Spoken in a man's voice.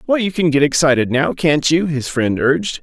Yes: male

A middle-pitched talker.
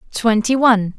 No: high, 225 Hz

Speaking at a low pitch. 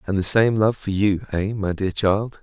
Yes: low, 100 Hz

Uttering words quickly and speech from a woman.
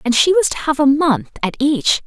Yes: fast, 260 wpm; female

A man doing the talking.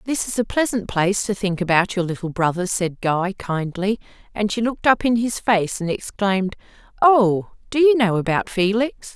No: female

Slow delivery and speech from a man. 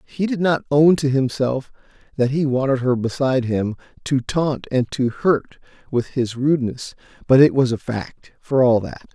No: average, 185 wpm; male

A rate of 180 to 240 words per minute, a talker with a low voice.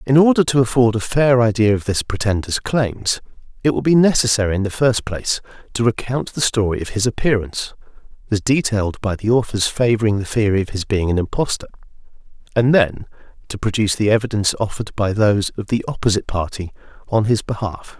Yes: average, 185 wpm; low, 110 Hz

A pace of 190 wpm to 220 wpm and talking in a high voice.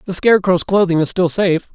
No: fast, 205 wpm; medium, 180 Hz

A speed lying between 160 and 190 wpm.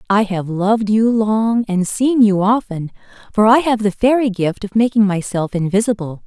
Yes: average, 180 wpm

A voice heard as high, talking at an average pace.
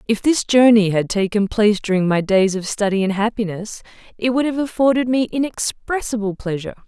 Yes: high, 215 Hz; average, 175 wpm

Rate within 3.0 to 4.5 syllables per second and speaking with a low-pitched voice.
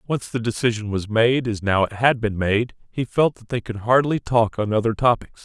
No: 5.1 syllables/s; low, 115 Hz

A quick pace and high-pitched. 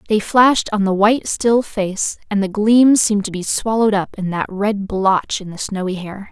Yes: fast, 220 wpm; high, 205 Hz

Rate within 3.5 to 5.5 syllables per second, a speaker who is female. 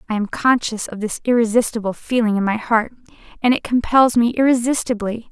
No: 5.7 syllables/s; female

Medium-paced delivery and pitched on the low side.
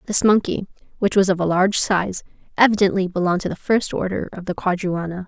No: average, 195 wpm; high, 190 Hz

